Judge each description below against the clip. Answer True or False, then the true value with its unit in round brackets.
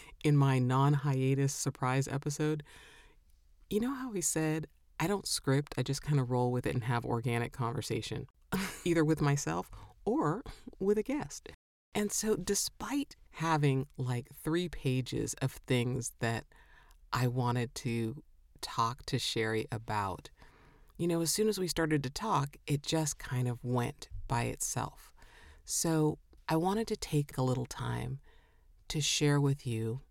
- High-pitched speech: False (135 Hz)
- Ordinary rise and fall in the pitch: True (4.6 semitones)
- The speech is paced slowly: False (155 wpm)